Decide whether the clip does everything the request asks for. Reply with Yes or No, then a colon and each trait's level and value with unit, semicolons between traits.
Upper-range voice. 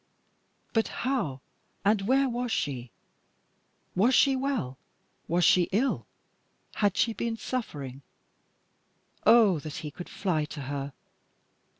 Yes: high, 195 Hz